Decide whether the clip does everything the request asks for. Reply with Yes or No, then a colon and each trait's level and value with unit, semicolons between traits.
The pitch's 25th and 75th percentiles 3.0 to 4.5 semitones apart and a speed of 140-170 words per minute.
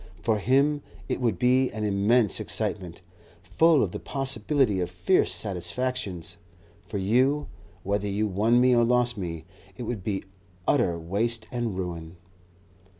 No: average, 5.1 semitones; average, 145 wpm